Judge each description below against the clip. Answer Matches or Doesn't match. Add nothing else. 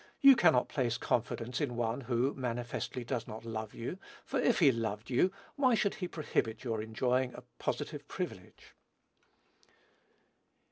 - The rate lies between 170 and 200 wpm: Doesn't match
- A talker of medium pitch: Doesn't match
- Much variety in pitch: Doesn't match